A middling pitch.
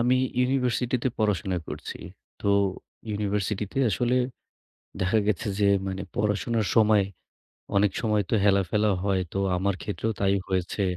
No: low, 105 Hz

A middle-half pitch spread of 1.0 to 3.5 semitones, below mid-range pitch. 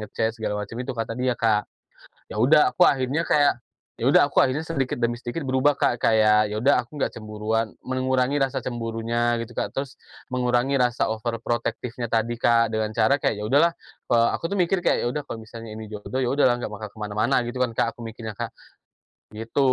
Yes: average, 2.8 semitones; low, 120 Hz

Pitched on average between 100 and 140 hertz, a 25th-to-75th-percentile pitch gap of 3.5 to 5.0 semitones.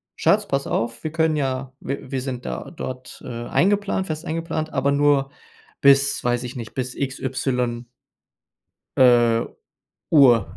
No: low, 135 Hz; average, 2.9 semitones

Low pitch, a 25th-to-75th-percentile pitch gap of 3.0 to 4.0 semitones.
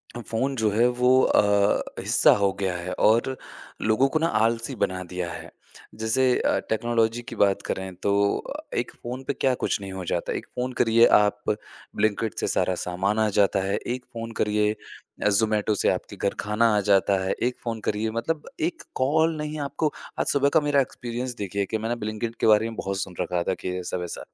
Yes: low, 110 Hz; average, 3.5 semitones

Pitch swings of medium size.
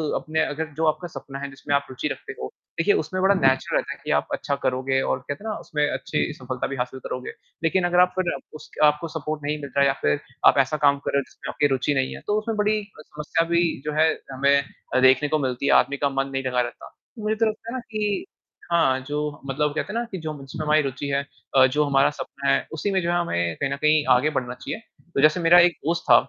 Yes: average, 3.9 semitones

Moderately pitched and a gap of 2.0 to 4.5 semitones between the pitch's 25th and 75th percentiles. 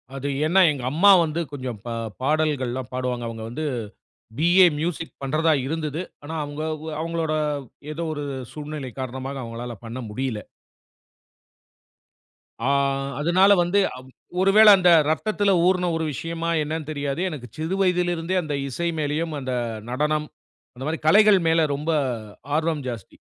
Yes: medium, 155 Hz; average, 4.0 semitones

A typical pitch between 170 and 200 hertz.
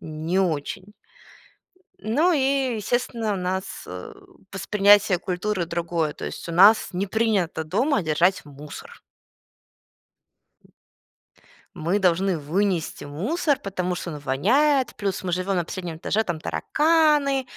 Yes: high, 190 Hz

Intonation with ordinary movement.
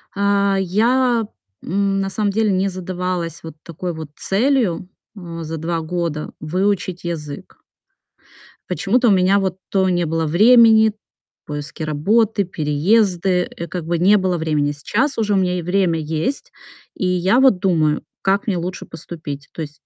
Yes: average, 3.5 semitones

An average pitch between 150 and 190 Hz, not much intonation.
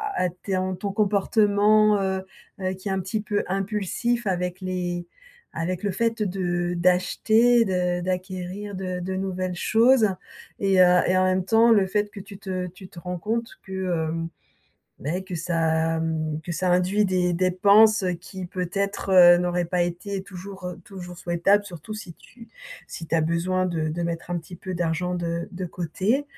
Yes: medium, 185 Hz; narrow, 2.3 semitones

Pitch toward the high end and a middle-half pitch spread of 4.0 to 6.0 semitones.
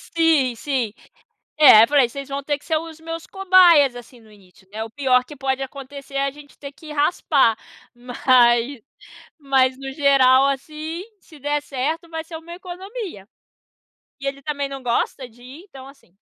No: very high, 275 Hz; average, 3.3 semitones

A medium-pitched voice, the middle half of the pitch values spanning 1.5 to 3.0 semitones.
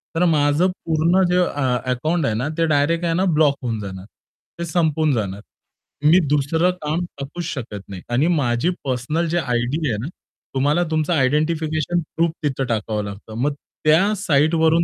No: medium, 150 Hz; average, 4.7 semitones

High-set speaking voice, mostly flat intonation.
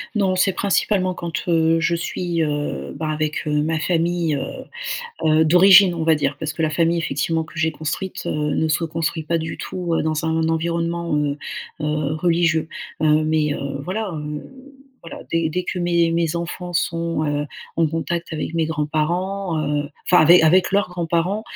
No: medium, 165 Hz; narrow, 1.9 semitones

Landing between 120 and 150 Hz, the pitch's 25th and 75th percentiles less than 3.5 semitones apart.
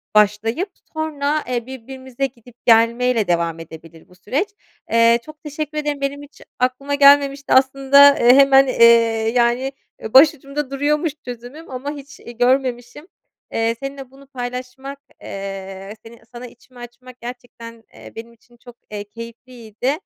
No: very high, 255 Hz; average, 3.1 semitones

